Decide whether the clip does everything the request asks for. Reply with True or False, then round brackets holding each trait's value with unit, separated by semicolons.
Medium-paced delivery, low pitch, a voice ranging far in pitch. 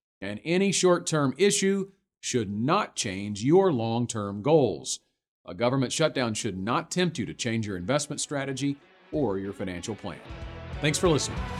True (160 wpm; 125 Hz; 7.7 semitones)